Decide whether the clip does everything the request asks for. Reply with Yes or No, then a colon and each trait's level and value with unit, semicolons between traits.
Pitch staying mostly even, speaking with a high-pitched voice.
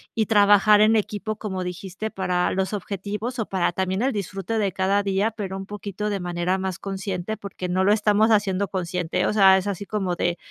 Yes: narrow, 2.0 semitones; high, 195 Hz